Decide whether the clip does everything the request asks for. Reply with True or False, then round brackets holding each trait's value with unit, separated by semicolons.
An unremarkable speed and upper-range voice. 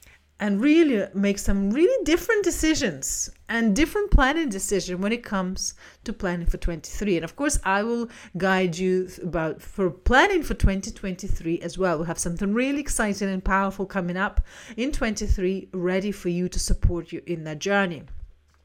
True (165 wpm; 195 Hz)